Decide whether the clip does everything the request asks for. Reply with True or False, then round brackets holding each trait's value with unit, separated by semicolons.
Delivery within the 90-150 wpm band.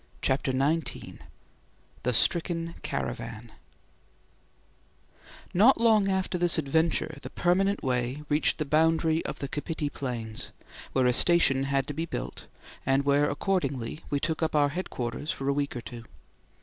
True (145 wpm)